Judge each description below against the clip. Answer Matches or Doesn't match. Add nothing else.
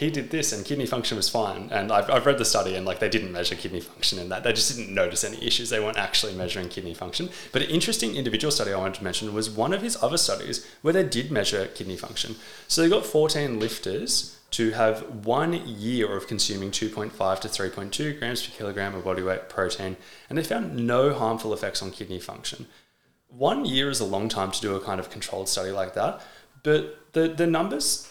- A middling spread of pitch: Doesn't match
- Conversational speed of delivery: Doesn't match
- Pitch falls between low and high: Doesn't match